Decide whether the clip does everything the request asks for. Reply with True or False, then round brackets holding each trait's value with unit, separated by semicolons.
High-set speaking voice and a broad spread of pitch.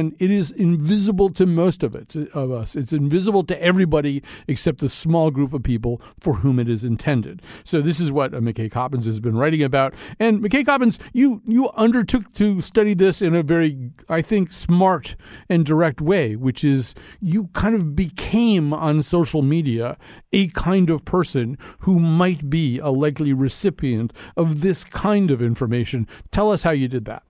False (160 Hz; 5.9 semitones)